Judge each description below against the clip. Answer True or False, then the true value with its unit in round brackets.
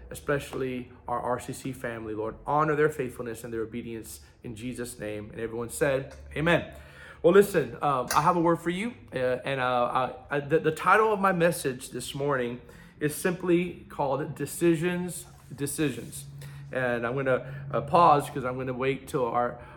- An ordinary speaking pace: True (175 wpm)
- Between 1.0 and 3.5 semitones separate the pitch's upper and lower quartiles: False (3.9 semitones)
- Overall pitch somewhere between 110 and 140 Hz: True (135 Hz)